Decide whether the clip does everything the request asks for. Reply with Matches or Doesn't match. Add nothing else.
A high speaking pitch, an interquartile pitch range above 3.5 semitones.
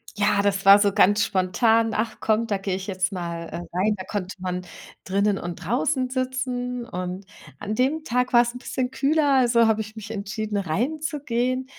Matches